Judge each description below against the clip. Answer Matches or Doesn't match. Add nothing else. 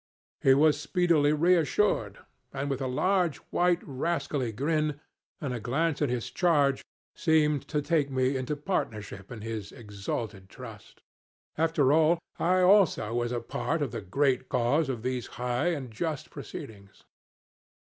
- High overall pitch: Doesn't match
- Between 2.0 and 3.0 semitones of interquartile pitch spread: Doesn't match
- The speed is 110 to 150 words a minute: Matches